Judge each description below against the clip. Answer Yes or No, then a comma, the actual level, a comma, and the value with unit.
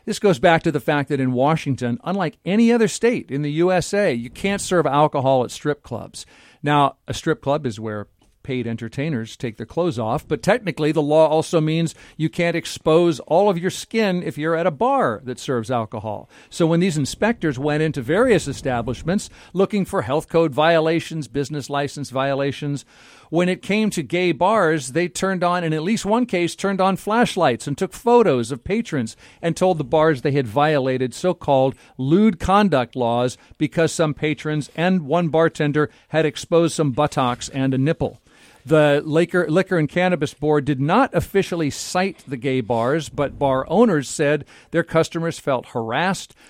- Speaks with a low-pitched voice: No, medium, 155 Hz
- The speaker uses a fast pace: No, average, 180 wpm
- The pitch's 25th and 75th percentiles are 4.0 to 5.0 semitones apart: Yes, average, 4.4 semitones